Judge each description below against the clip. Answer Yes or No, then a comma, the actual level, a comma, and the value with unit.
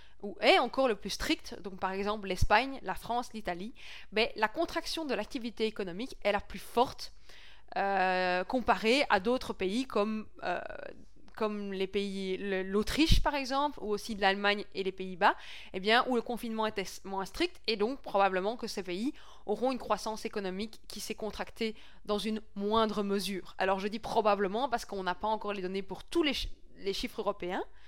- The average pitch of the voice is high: Yes, high, 210 Hz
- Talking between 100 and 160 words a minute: No, average, 185 wpm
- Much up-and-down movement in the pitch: No, average, 3.2 semitones